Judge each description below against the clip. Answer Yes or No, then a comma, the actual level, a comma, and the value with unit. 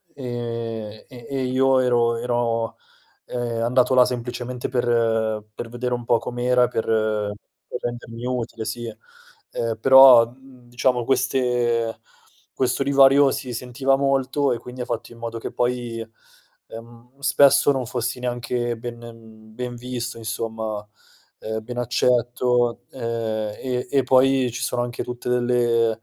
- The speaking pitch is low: Yes, low, 120 Hz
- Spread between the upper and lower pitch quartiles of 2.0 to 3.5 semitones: No, narrow, 1.5 semitones